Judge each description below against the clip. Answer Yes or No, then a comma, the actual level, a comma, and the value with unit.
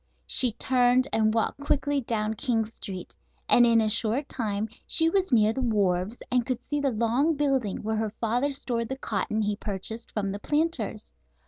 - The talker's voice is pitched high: Yes, high, 230 Hz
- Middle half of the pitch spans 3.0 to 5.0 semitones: Yes, average, 3.7 semitones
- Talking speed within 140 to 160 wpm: No, average, 185 wpm